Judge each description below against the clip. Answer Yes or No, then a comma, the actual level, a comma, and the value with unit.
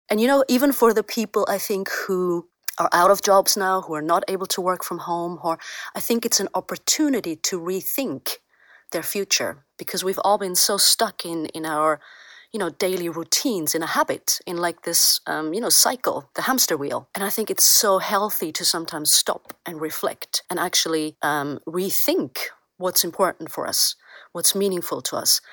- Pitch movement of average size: Yes, average, 3.5 semitones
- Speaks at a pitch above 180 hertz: Yes, high, 190 Hz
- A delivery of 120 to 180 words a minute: No, average, 195 wpm